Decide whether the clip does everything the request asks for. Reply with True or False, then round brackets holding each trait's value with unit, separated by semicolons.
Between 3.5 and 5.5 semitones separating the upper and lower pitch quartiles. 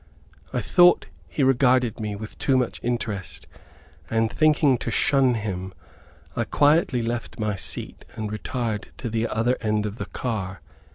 False (3.1 semitones)